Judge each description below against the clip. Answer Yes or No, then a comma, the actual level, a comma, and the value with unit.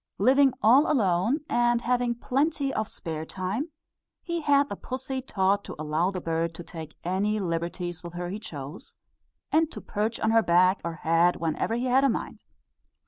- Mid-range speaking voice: No, high, 205 Hz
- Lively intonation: Yes, wide, 6.9 semitones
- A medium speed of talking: Yes, average, 180 wpm